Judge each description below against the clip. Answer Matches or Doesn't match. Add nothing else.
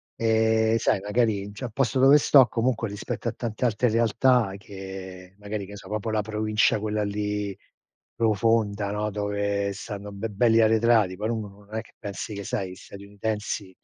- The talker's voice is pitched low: Matches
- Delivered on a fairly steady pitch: Matches